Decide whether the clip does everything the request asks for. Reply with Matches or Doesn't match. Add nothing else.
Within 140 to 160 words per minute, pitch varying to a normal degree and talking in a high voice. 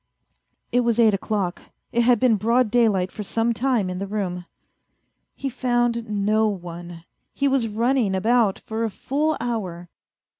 Matches